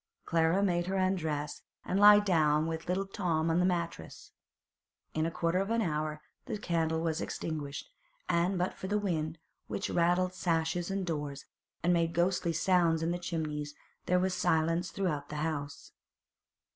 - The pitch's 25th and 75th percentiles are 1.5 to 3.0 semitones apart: Yes, narrow, 2.5 semitones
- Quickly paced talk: No, average, 165 wpm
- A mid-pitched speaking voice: Yes, medium, 170 Hz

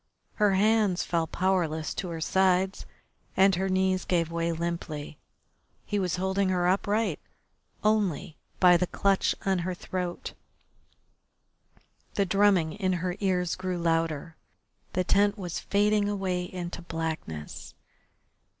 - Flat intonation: Yes, narrow, 2.3 semitones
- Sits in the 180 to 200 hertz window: Yes, medium, 185 Hz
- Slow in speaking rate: Yes, slow, 125 wpm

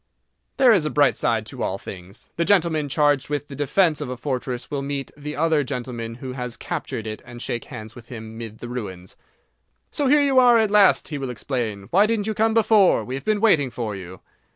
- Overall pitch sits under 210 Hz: Yes, medium, 140 Hz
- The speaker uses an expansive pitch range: Yes, wide, 7.7 semitones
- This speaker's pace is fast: Yes, fast, 225 wpm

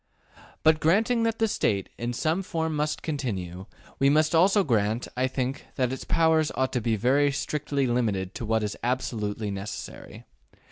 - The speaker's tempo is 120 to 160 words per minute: No, average, 170 wpm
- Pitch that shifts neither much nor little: No, wide, 6.0 semitones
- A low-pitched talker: Yes, low, 130 Hz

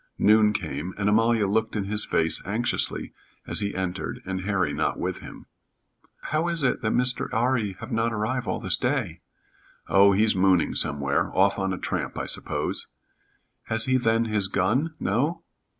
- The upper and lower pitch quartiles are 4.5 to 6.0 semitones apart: No, average, 3.4 semitones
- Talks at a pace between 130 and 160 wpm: No, average, 170 wpm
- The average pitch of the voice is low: Yes, low, 105 Hz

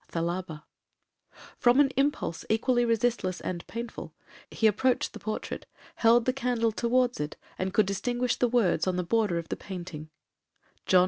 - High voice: Yes, high, 225 Hz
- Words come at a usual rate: Yes, average, 150 wpm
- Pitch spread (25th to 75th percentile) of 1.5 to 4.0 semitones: No, average, 5.0 semitones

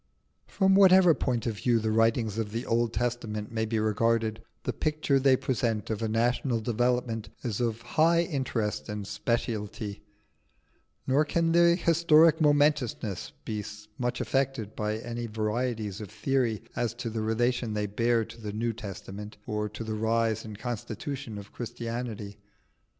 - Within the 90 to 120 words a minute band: No, average, 155 wpm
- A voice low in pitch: Yes, low, 115 Hz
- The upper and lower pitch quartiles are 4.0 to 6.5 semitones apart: No, average, 2.8 semitones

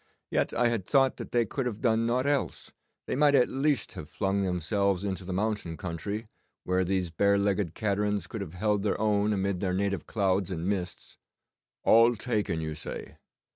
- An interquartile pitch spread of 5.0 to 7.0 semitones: No, average, 3.3 semitones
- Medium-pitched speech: No, low, 100 Hz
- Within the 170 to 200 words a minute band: Yes, average, 185 wpm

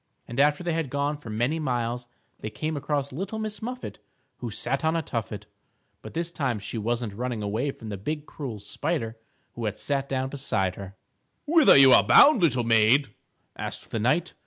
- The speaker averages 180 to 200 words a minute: Yes, average, 190 wpm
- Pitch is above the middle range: No, low, 135 Hz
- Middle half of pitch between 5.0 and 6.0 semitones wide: Yes, wide, 5.4 semitones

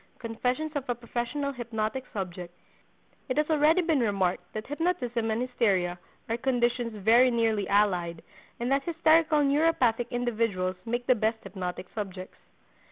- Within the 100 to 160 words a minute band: Yes, average, 140 wpm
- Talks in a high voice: Yes, high, 235 Hz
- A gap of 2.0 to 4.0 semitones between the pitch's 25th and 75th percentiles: No, average, 4.4 semitones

